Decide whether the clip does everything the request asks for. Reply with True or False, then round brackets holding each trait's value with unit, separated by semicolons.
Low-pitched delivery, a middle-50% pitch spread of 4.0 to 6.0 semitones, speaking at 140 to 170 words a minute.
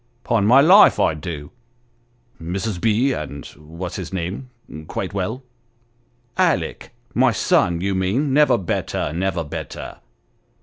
True (100 Hz; 5.6 semitones; 155 wpm)